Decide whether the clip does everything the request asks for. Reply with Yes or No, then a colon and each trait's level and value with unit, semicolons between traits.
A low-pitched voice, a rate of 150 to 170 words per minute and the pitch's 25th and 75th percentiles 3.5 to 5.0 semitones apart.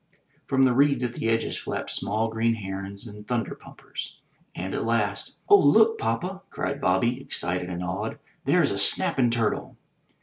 Yes: low, 115 Hz; average, 165 wpm; average, 4.7 semitones